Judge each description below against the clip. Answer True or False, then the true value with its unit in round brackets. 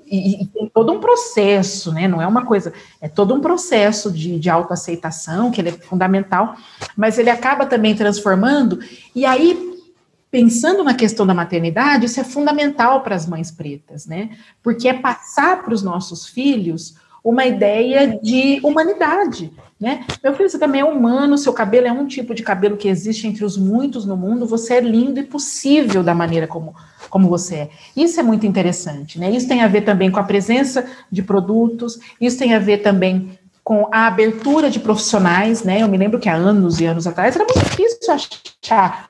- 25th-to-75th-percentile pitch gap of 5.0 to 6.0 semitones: True (5.5 semitones)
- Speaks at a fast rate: True (190 wpm)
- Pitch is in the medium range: False (220 Hz)